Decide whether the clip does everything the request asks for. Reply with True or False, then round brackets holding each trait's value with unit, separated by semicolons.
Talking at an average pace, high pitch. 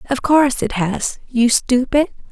True (155 wpm; 255 Hz)